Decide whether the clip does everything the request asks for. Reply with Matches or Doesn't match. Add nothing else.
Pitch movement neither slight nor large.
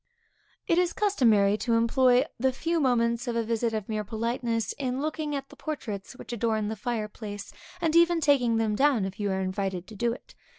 Matches